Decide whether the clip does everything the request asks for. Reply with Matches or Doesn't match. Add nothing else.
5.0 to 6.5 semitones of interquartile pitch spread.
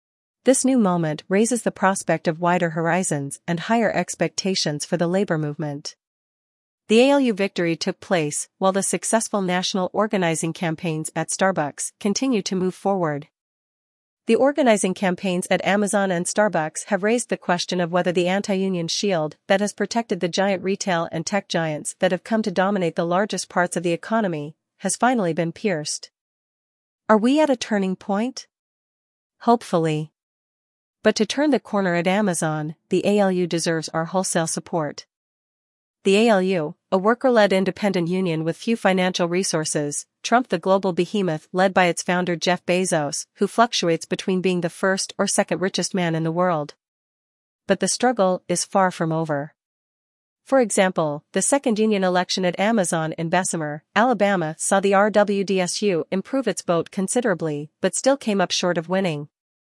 Doesn't match